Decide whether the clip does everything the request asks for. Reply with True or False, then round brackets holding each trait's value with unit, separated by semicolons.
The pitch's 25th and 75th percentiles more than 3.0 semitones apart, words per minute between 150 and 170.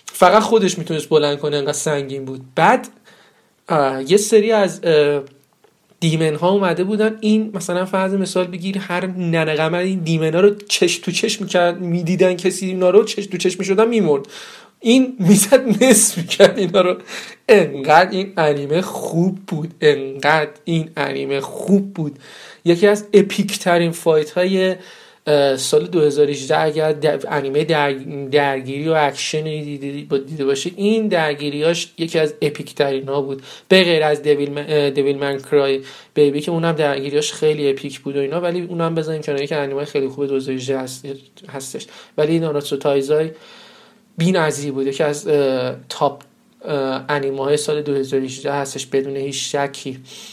True (4.5 semitones; 155 wpm)